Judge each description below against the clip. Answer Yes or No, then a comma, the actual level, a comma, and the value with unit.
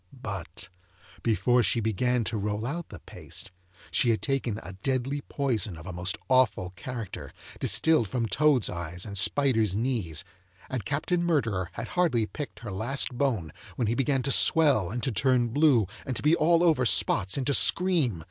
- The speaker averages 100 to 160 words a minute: No, average, 175 wpm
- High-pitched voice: No, low, 120 Hz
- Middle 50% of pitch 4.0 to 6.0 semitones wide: Yes, average, 5.1 semitones